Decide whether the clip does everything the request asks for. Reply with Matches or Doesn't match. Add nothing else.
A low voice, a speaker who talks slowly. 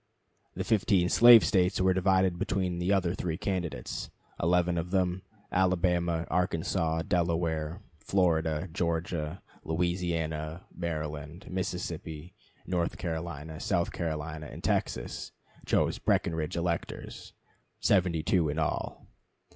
Matches